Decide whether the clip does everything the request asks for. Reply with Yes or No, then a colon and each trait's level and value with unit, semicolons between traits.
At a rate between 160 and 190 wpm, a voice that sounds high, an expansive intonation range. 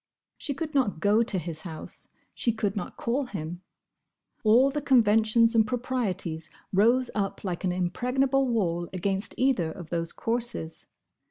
No: average, 150 wpm; high, 215 Hz; wide, 5.8 semitones